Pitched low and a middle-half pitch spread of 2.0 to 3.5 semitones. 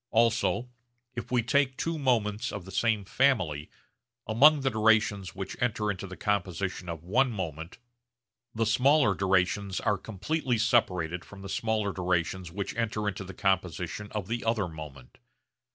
No: low, 105 Hz; average, 3.9 semitones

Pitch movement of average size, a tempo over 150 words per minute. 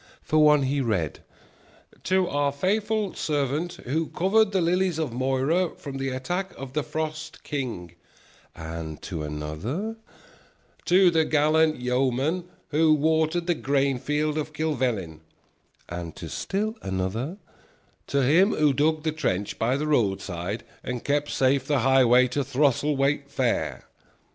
No: average, 4.2 semitones; average, 140 wpm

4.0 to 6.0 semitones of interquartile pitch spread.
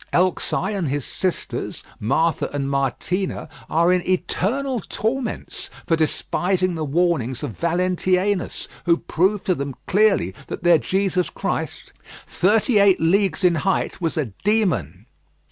No: average, 3.4 semitones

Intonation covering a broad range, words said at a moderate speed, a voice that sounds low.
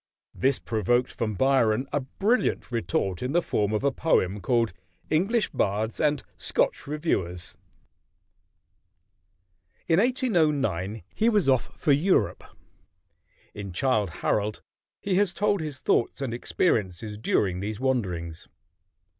No: wide, 7.1 semitones; slow, 120 wpm; low, 125 Hz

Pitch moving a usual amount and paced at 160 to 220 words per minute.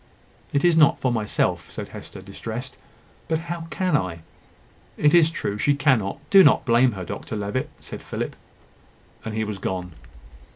No: wide, 7.5 semitones; average, 165 wpm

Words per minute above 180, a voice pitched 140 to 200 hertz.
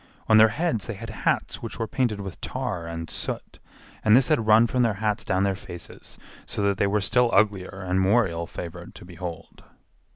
No: fast, 205 wpm; low, 105 Hz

